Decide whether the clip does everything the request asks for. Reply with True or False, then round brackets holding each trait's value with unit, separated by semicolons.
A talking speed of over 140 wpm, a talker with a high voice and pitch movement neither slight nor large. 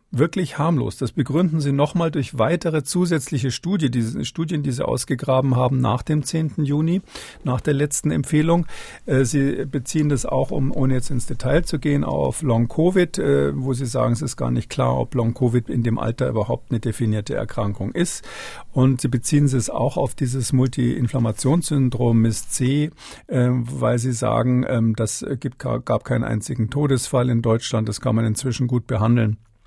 False (165 wpm; 130 Hz; 3.6 semitones)